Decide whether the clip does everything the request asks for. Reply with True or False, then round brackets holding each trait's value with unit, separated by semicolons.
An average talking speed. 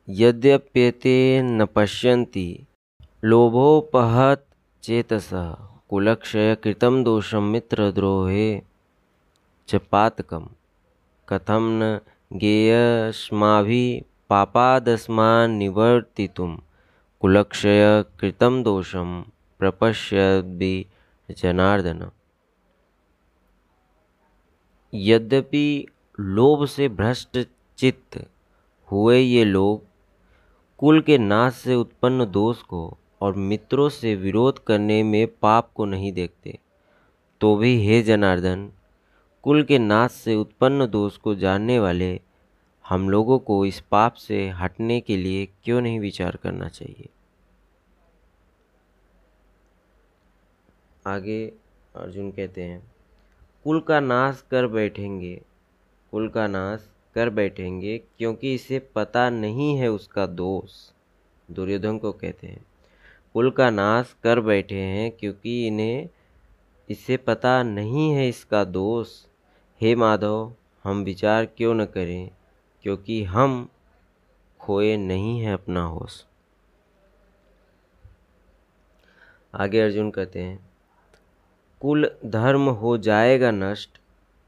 False (90 wpm)